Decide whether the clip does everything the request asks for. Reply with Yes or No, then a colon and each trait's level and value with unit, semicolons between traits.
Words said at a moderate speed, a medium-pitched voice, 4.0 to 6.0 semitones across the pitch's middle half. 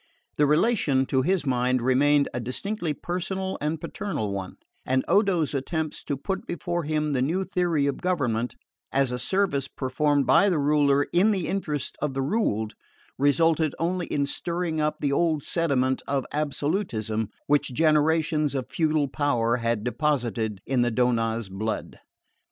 Yes: average, 155 wpm; medium, 145 Hz; average, 4.6 semitones